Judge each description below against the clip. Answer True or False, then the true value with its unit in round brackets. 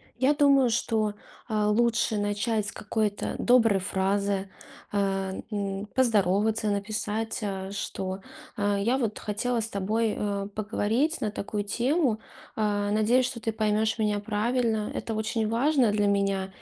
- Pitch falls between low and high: False (215 Hz)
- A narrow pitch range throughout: True (2.1 semitones)